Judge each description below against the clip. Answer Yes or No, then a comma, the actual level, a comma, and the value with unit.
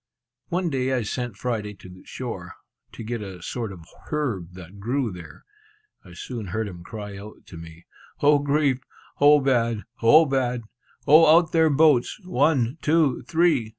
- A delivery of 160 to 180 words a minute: Yes, average, 165 wpm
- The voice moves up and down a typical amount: No, wide, 6.1 semitones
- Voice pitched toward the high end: No, low, 125 Hz